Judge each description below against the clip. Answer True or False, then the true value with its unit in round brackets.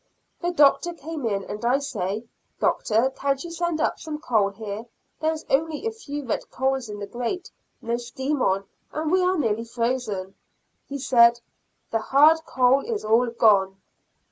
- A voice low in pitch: False (255 Hz)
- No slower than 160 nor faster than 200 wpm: True (170 wpm)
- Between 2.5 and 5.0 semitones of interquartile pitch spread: False (5.5 semitones)